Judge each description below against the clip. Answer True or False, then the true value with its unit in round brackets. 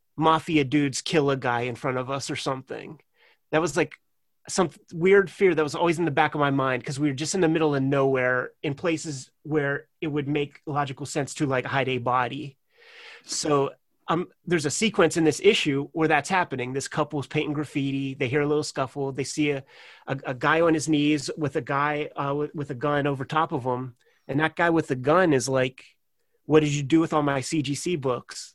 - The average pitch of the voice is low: False (145 Hz)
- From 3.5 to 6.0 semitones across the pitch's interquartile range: False (2.5 semitones)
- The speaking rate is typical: False (225 wpm)